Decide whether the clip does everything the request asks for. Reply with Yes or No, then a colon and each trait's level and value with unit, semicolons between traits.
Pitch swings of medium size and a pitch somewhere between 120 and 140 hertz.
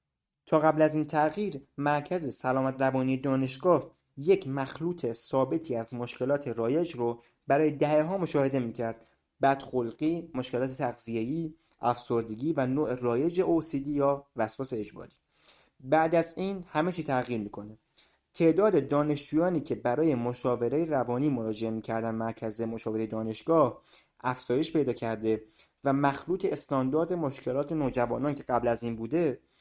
Yes: average, 4.6 semitones; low, 135 Hz